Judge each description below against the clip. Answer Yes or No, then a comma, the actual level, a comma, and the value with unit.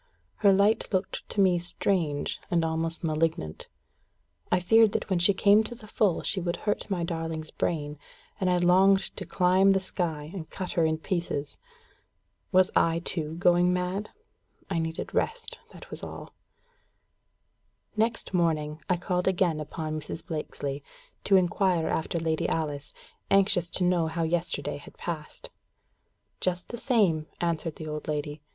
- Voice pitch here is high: No, medium, 175 Hz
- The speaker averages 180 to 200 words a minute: No, average, 155 wpm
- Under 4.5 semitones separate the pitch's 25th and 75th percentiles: Yes, average, 3.1 semitones